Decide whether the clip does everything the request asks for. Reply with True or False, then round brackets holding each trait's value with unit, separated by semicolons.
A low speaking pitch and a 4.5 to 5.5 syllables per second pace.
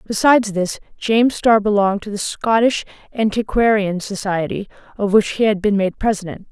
False (205 Hz; 5.3 syllables/s)